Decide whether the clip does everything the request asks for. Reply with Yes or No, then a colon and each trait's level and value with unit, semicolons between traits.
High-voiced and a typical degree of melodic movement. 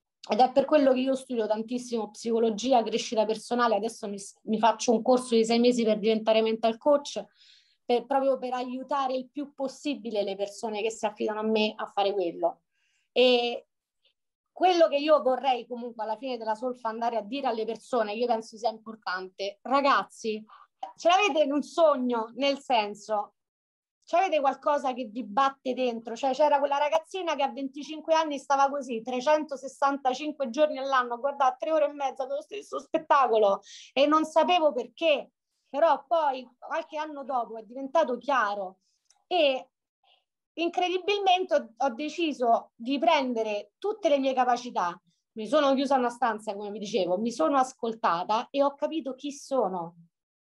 Yes: very high, 255 Hz; average, 4.6 semitones